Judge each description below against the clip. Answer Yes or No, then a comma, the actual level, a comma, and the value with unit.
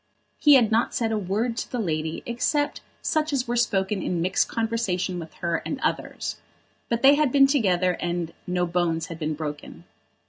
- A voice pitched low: No, high, 195 Hz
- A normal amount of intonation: No, wide, 5.7 semitones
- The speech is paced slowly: No, average, 185 wpm